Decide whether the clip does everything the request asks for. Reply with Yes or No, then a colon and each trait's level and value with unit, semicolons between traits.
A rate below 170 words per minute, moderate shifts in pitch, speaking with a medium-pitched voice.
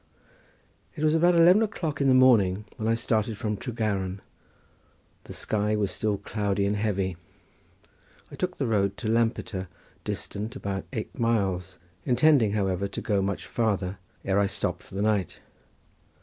No: average, 155 wpm; average, 3.0 semitones; low, 105 Hz